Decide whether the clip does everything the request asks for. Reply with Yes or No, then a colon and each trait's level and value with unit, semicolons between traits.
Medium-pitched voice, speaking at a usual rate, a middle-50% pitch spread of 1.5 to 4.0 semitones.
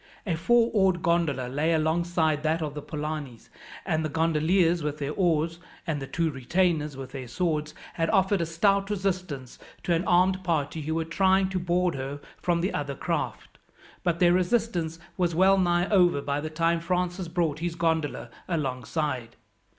Yes: medium, 165 Hz; average, 175 wpm; average, 3.1 semitones